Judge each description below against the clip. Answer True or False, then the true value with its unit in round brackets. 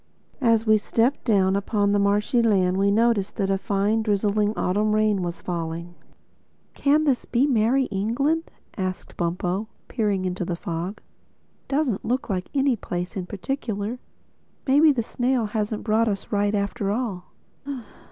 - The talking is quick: False (145 wpm)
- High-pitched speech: True (210 Hz)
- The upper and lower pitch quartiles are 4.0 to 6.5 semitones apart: False (3.4 semitones)